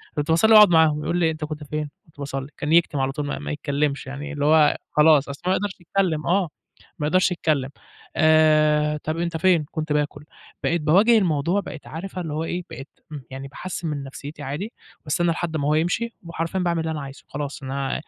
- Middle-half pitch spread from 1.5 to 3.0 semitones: Yes, average, 2.7 semitones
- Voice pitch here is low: No, medium, 155 Hz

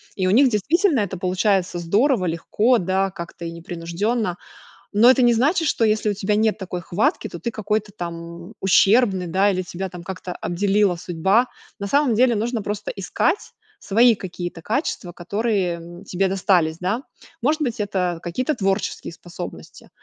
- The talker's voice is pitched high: Yes, high, 195 Hz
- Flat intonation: No, average, 4.2 semitones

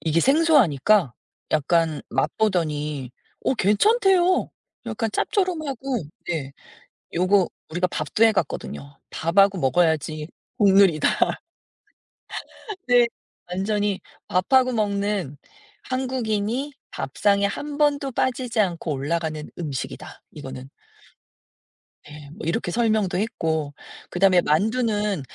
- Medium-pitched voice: No, high, 195 Hz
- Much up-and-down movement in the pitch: Yes, wide, 6.9 semitones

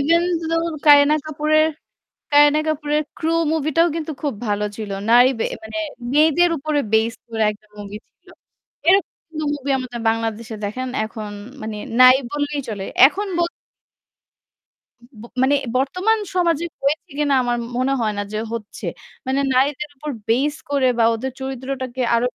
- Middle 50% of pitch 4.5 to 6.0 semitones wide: Yes, average, 4.8 semitones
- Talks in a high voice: Yes, very high, 275 Hz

